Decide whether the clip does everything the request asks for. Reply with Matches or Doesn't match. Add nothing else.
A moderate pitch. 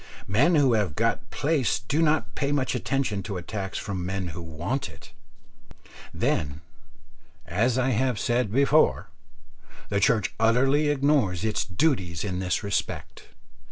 Doesn't match